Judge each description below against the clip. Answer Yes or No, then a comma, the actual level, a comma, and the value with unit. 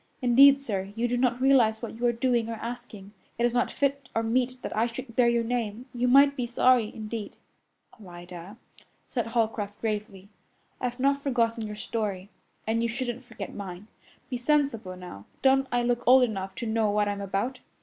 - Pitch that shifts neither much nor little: Yes, average, 3.0 semitones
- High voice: Yes, high, 235 Hz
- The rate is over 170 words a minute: Yes, average, 190 wpm